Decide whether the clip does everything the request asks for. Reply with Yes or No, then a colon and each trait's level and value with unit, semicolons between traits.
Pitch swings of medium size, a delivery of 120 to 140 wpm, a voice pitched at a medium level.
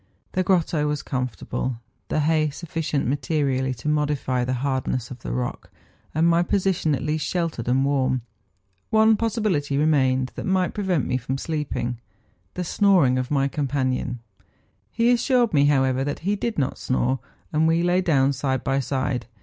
No: average, 4.5 semitones; average, 165 wpm; medium, 145 Hz